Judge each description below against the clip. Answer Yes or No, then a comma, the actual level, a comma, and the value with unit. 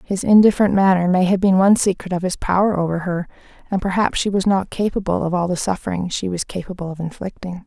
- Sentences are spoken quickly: Yes, fast, 220 wpm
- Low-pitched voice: No, medium, 185 Hz